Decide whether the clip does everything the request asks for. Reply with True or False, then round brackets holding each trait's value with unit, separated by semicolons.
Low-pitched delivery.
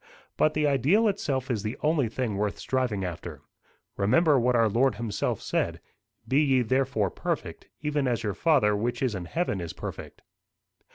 True (125 Hz)